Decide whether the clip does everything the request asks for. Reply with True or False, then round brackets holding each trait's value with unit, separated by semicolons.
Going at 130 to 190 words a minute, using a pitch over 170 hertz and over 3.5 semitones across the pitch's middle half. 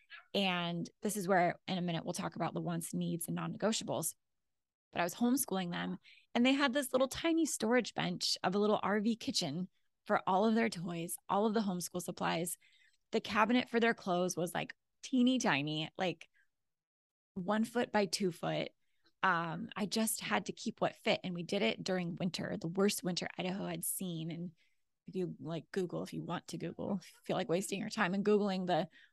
False (200 wpm; 190 Hz; 3.9 semitones)